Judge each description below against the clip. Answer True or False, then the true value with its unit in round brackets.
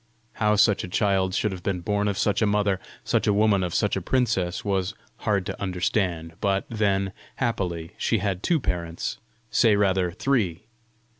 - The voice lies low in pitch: True (100 Hz)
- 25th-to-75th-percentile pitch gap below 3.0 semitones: True (2.6 semitones)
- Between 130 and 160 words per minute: False (175 wpm)